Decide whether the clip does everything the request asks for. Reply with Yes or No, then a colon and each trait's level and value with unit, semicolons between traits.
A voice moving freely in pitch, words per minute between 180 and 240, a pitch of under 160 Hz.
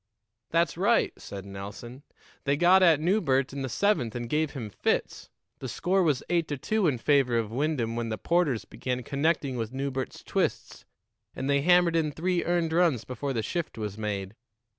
Yes: wide, 6.2 semitones; average, 185 wpm; medium, 140 Hz